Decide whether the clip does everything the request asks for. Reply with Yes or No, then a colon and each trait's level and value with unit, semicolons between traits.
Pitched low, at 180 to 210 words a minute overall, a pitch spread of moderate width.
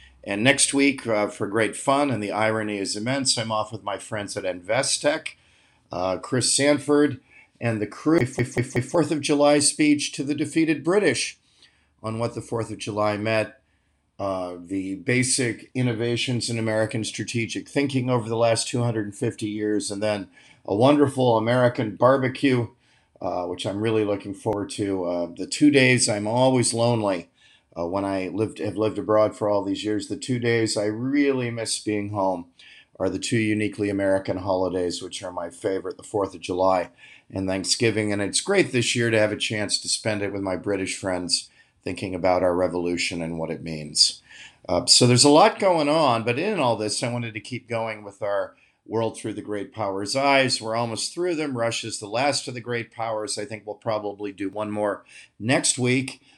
Yes: low, 110 Hz; average, 190 wpm; average, 3.8 semitones